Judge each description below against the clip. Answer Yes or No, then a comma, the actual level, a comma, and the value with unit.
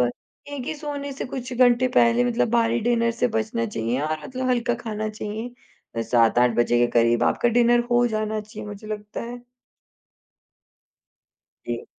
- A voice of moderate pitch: No, high, 230 Hz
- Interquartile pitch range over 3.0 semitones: No, narrow, 2.6 semitones